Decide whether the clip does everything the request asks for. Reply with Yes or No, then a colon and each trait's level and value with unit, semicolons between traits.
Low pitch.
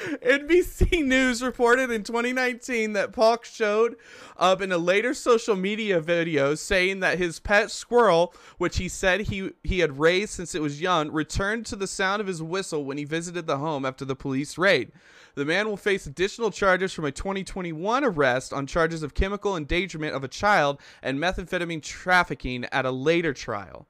No: medium, 185 Hz